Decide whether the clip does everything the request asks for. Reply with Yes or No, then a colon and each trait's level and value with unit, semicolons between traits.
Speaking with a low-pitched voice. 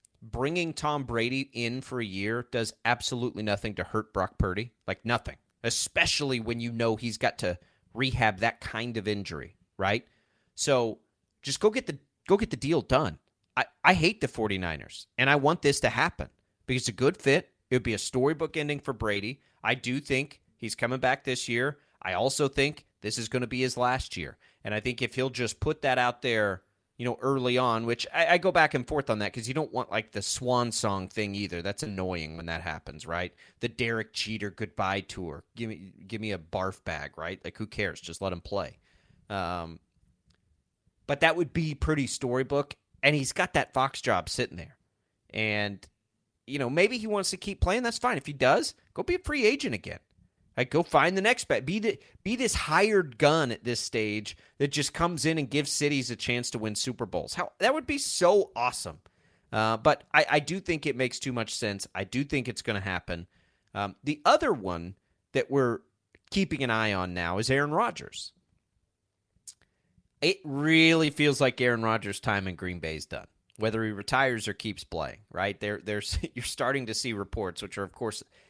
Yes: low, 115 Hz